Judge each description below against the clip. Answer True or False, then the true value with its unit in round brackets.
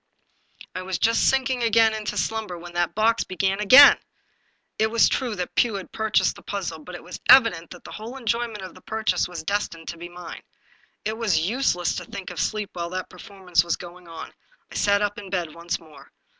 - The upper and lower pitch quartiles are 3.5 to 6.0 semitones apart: True (4.1 semitones)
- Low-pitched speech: False (195 Hz)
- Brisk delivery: True (210 wpm)